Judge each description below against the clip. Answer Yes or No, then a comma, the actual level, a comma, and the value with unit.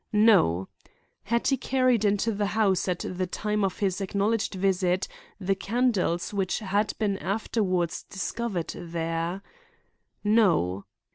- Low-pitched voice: No, high, 195 Hz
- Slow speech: Yes, slow, 125 wpm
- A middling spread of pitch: Yes, average, 3.0 semitones